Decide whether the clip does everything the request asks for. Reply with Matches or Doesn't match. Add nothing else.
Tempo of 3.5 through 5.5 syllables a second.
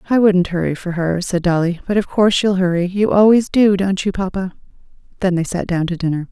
Doesn't match